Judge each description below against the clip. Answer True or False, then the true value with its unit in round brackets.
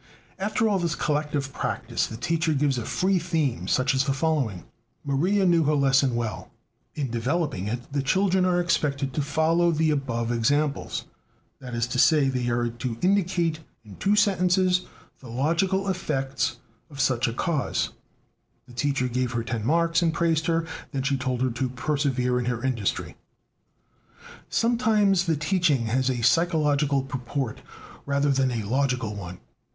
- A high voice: False (140 Hz)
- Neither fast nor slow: True (160 wpm)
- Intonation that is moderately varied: True (5.0 semitones)